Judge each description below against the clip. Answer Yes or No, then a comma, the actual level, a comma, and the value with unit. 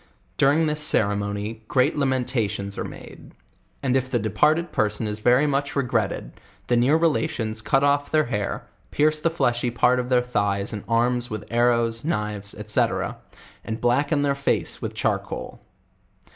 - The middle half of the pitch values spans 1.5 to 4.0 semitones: No, average, 4.6 semitones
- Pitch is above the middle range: No, low, 125 Hz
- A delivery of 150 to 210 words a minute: Yes, average, 160 wpm